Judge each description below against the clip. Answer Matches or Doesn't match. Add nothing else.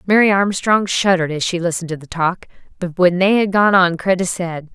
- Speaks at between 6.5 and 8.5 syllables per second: Doesn't match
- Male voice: Doesn't match